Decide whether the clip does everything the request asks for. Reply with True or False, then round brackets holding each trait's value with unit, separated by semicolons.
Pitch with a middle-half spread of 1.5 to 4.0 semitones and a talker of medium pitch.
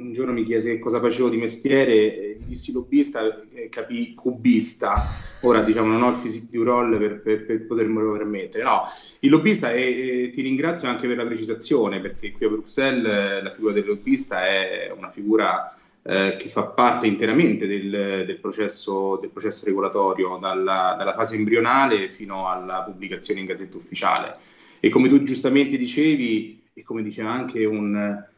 False (3.3 semitones; 115 Hz)